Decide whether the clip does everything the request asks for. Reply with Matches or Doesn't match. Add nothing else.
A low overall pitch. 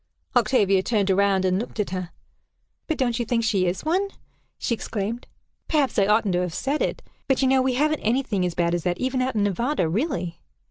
Doesn't match